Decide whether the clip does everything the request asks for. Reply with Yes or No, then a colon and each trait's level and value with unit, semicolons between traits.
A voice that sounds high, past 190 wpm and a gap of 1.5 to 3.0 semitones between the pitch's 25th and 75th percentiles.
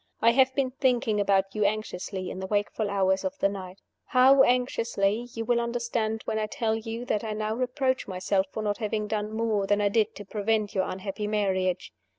Yes: high, 215 Hz; average, 200 wpm; average, 2.7 semitones